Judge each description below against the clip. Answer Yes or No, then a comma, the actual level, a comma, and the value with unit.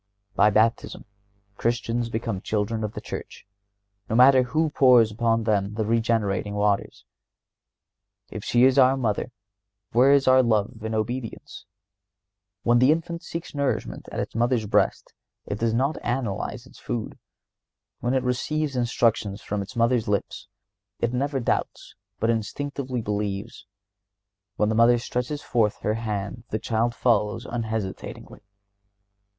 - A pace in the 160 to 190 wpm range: No, average, 140 wpm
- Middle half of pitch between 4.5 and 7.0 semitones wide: No, average, 2.9 semitones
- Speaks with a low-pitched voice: Yes, low, 115 Hz